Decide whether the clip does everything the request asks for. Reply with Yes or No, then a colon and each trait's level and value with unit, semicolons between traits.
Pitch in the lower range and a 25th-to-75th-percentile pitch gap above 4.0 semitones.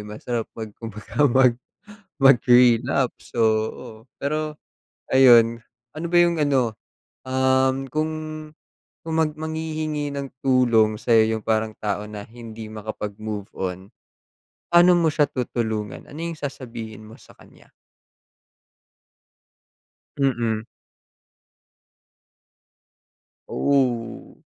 Yes: low, 125 Hz; average, 4.5 semitones